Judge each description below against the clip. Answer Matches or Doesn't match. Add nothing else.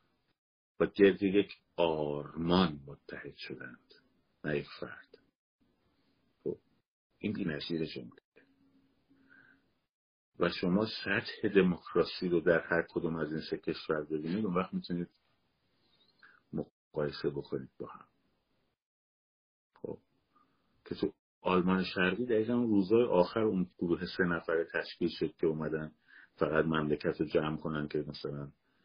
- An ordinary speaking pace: Matches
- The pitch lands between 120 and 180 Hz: Doesn't match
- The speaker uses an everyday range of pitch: Matches